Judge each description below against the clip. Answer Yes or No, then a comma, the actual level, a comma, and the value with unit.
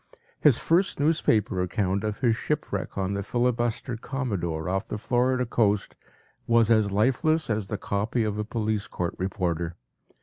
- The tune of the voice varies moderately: Yes, average, 3.8 semitones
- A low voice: Yes, low, 110 Hz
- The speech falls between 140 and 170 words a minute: Yes, average, 155 wpm